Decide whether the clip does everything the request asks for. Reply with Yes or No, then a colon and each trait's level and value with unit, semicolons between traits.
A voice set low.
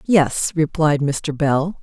No: medium, 155 Hz